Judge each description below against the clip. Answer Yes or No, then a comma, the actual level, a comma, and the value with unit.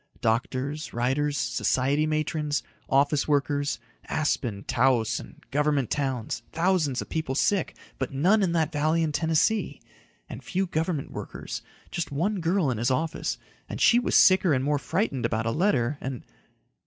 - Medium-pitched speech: Yes, medium, 145 Hz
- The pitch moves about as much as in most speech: Yes, average, 3.9 semitones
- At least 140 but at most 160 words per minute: Yes, average, 155 wpm